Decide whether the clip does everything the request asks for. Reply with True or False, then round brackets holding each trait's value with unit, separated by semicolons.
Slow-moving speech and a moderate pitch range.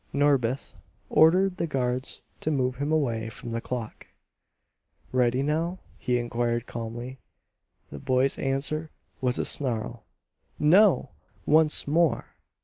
True (120 wpm; 4.2 semitones)